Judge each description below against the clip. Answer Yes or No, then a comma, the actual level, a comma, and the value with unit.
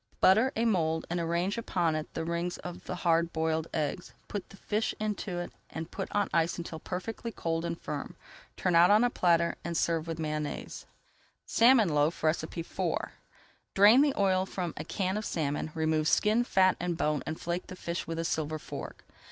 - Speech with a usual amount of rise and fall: Yes, average, 3.1 semitones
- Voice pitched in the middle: Yes, medium, 170 Hz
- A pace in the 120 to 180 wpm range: No, average, 190 wpm